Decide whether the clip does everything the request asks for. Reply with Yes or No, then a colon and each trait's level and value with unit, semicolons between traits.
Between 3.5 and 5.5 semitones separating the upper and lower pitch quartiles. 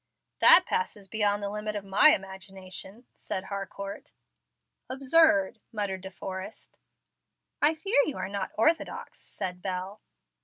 No: average, 3.0 semitones